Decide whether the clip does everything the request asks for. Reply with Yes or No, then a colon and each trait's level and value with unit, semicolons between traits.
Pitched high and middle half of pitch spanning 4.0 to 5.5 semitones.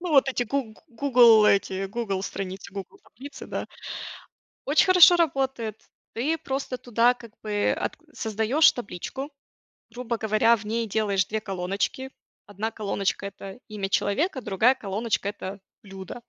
Yes: high, 220 Hz; average, 4.4 semitones